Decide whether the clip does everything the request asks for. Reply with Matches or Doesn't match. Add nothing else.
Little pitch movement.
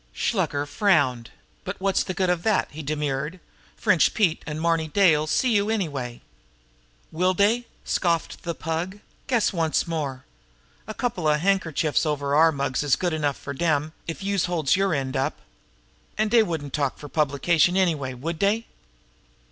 Doesn't match